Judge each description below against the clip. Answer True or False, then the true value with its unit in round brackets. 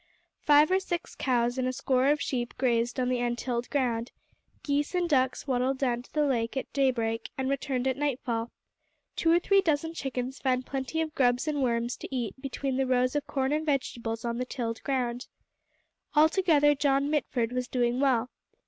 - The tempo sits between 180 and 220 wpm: True (185 wpm)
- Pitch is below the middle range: False (260 Hz)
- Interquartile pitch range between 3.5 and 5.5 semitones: False (2.9 semitones)